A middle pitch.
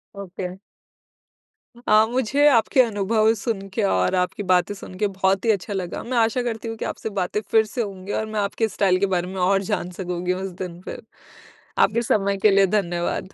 No: high, 200 Hz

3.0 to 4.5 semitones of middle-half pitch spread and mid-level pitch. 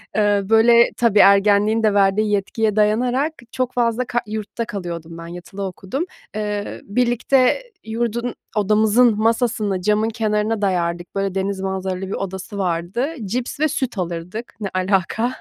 No: average, 3.3 semitones; high, 210 Hz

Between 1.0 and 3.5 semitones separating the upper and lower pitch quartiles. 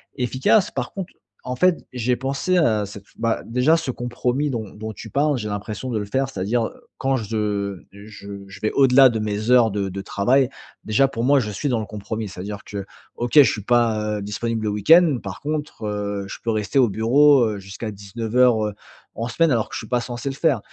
No: average, 4.1 semitones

